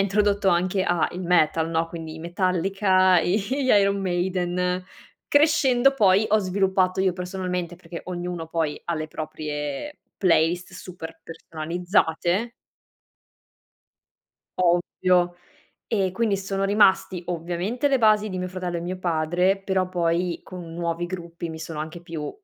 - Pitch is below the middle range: No, medium, 180 Hz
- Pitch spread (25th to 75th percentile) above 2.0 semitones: Yes, narrow, 2.4 semitones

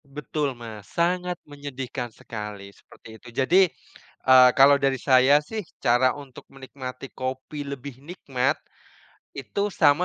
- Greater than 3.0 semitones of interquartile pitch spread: No, narrow, 2.4 semitones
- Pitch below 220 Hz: Yes, low, 135 Hz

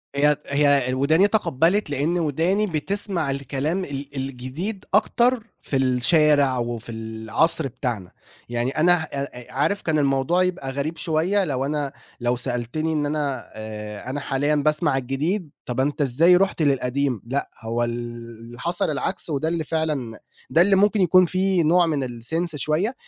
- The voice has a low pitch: No, medium, 145 Hz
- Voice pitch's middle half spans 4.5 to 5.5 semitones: Yes, average, 4.8 semitones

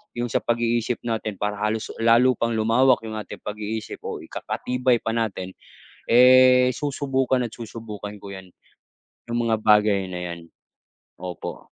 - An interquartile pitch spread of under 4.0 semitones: Yes, average, 2.8 semitones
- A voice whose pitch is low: Yes, low, 115 Hz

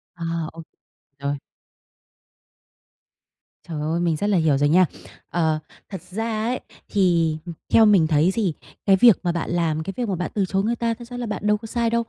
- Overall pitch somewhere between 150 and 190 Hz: Yes, medium, 185 Hz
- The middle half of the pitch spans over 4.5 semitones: Yes, average, 5.0 semitones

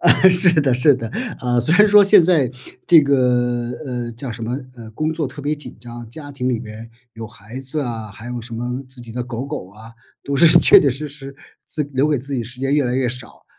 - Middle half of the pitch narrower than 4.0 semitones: Yes, average, 3.4 semitones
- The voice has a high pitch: No, low, 125 Hz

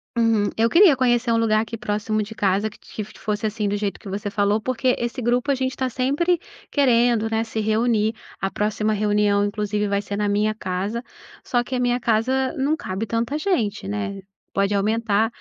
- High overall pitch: Yes, high, 220 Hz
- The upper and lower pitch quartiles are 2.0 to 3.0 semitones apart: Yes, average, 2.7 semitones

